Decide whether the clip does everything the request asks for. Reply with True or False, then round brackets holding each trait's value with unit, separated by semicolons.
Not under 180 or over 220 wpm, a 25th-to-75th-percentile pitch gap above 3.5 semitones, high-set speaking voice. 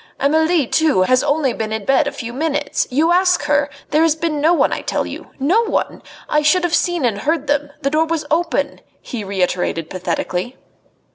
True (200 wpm; 4.5 semitones; 290 Hz)